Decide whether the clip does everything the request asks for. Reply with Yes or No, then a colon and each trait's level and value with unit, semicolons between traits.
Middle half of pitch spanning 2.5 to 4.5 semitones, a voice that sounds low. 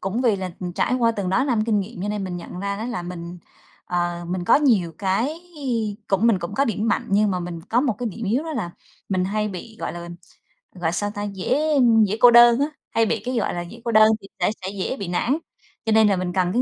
No: average, 4.2 semitones; high, 205 Hz